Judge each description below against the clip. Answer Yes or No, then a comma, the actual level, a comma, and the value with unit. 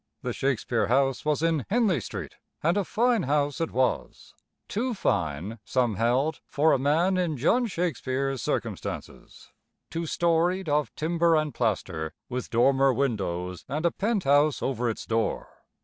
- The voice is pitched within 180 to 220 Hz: No, medium, 145 Hz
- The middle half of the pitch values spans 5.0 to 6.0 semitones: Yes, wide, 5.6 semitones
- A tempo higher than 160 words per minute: No, average, 150 wpm